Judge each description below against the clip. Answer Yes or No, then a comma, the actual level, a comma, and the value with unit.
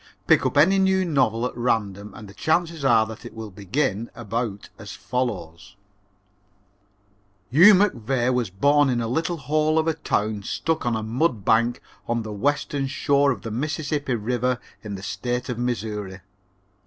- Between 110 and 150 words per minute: No, average, 165 wpm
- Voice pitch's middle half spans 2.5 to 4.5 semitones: No, average, 5.1 semitones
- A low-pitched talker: Yes, low, 120 Hz